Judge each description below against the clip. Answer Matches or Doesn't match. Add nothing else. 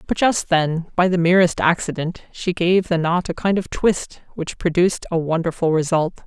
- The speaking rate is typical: Matches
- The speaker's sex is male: Doesn't match